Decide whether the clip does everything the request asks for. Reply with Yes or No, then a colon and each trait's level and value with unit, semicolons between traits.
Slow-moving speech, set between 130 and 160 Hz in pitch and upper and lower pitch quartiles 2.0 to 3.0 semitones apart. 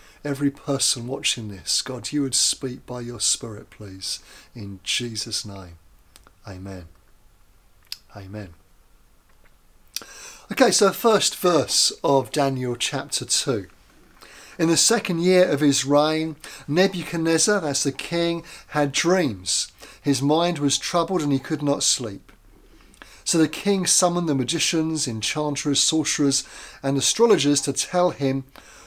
No: slow, 125 wpm; medium, 140 Hz; wide, 5.4 semitones